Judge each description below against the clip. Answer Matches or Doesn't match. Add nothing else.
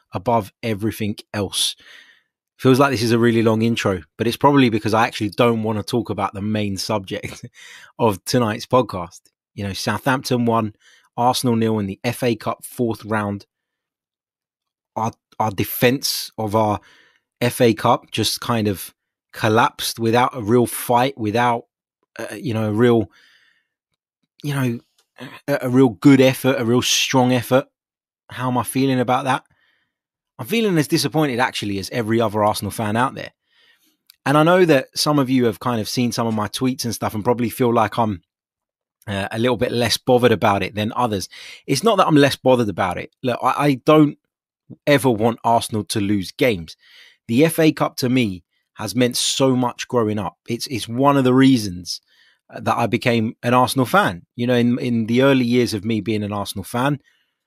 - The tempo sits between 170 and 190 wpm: Matches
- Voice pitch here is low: Matches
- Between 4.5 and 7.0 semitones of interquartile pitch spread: Doesn't match